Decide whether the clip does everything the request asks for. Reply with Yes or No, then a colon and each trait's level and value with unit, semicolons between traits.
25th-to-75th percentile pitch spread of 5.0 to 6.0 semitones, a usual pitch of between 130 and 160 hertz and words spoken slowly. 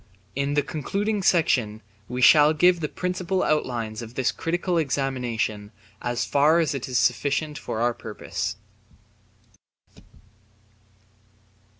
Yes: average, 5.3 semitones; medium, 140 Hz; slow, 110 wpm